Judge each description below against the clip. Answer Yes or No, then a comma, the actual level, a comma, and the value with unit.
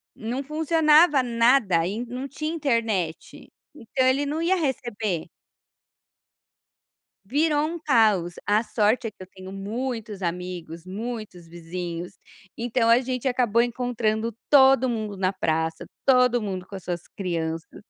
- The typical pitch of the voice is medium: No, high, 230 Hz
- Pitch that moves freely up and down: Yes, wide, 5.8 semitones